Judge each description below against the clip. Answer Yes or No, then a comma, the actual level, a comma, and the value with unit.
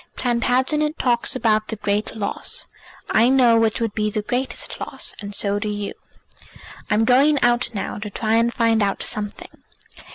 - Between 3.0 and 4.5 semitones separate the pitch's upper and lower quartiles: No, narrow, 2.6 semitones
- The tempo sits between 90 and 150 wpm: No, average, 165 wpm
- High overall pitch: Yes, high, 225 Hz